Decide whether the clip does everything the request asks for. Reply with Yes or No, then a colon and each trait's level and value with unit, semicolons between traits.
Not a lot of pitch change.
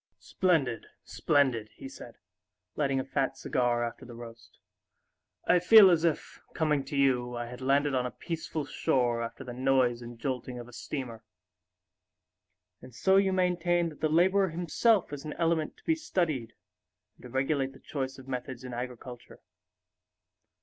No: average, 4.8 semitones